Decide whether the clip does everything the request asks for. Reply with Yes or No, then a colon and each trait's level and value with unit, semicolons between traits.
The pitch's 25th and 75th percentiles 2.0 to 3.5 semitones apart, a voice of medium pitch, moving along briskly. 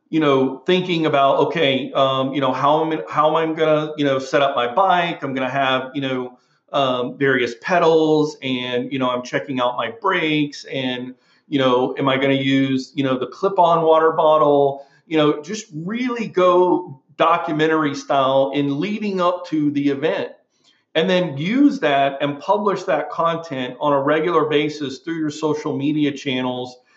No: average, 3.2 semitones; medium, 145 Hz; average, 185 wpm